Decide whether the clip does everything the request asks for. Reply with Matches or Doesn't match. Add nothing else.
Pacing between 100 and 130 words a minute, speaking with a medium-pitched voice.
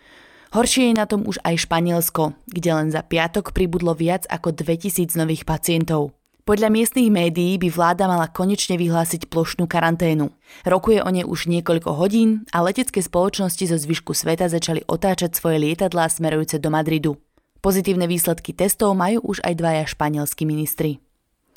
Doesn't match